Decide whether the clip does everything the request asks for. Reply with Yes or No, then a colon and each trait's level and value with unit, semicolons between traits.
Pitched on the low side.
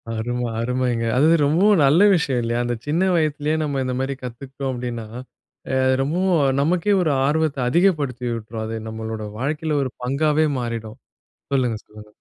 Yes: low, 130 Hz